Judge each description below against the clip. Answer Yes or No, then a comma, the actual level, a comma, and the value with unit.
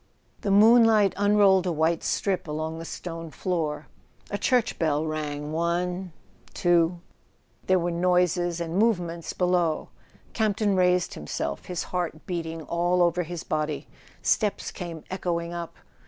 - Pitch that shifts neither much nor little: No, narrow, 2.2 semitones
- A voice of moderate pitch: Yes, medium, 175 Hz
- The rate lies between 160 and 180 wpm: No, slow, 135 wpm